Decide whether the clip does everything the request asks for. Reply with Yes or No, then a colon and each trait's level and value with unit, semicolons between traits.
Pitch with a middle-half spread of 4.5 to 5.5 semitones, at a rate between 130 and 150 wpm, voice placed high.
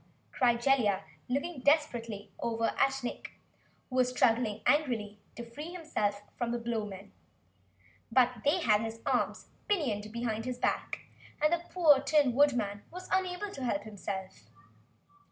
Yes: average, 5.0 semitones; average, 140 wpm; high, 245 Hz